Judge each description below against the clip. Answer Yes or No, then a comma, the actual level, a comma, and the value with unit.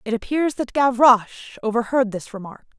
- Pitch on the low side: No, high, 240 Hz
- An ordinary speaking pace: Yes, average, 150 wpm